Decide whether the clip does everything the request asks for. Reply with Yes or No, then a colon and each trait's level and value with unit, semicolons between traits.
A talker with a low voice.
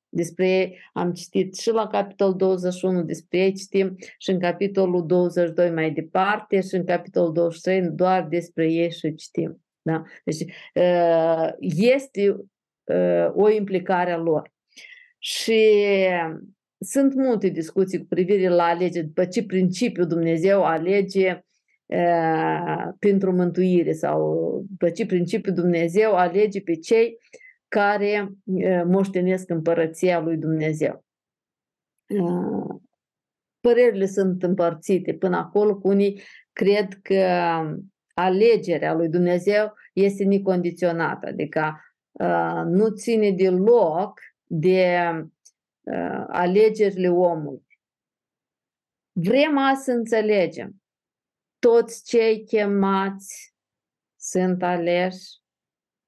No: medium, 185 Hz